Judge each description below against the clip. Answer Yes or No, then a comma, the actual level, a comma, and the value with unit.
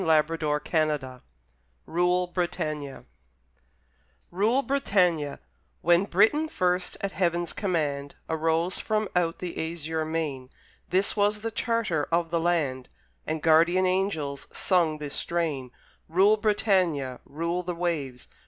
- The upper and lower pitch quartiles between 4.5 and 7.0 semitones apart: No, average, 3.3 semitones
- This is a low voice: No, medium, 170 Hz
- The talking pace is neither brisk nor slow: No, slow, 110 wpm